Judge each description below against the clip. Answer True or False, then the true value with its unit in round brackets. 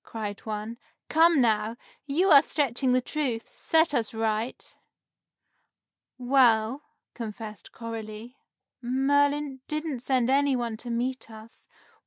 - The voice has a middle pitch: False (245 Hz)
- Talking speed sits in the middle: False (115 wpm)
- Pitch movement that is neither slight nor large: True (3.8 semitones)